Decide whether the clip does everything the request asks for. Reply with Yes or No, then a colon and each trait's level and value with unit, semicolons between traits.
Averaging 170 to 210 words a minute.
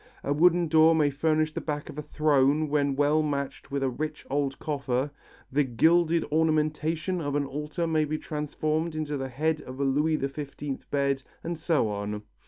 Yes: average, 185 wpm